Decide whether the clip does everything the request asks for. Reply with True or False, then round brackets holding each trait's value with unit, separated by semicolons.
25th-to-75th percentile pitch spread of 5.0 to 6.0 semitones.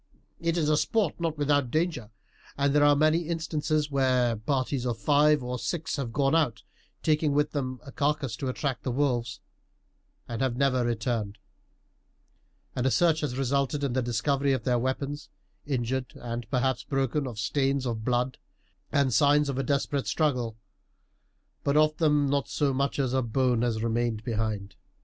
False (3.2 semitones)